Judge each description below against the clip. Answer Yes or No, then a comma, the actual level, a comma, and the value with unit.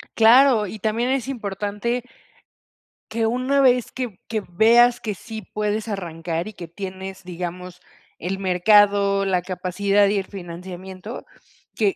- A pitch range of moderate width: Yes, average, 3.5 semitones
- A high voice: Yes, high, 200 Hz